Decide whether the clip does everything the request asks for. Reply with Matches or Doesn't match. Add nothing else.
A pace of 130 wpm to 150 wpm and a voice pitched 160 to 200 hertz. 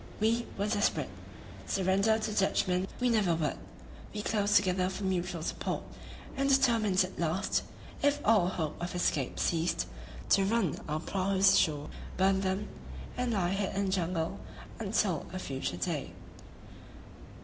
Matches